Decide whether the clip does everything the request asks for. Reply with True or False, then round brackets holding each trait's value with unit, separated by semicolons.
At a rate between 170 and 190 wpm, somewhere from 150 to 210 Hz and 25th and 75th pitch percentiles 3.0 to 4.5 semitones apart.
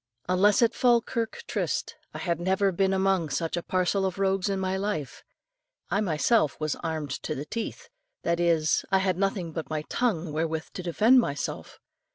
True (180 wpm; 185 Hz; 3.4 semitones)